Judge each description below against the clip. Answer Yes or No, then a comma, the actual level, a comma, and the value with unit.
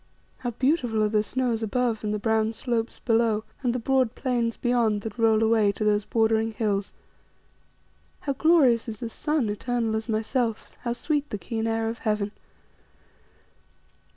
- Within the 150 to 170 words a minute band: Yes, average, 160 wpm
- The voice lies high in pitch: Yes, high, 225 Hz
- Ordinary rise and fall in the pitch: No, narrow, 2.0 semitones